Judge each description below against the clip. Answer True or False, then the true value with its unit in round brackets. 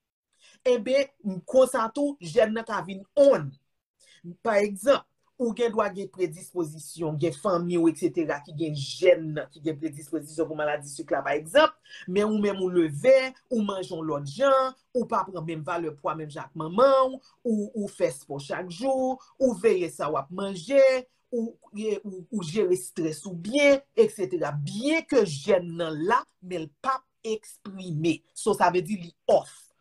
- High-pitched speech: True (195 Hz)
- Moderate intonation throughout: False (7.5 semitones)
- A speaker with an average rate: True (165 wpm)